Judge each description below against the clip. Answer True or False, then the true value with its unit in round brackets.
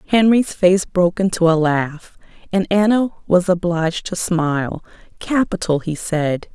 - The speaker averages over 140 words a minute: False (135 wpm)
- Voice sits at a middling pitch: True (180 Hz)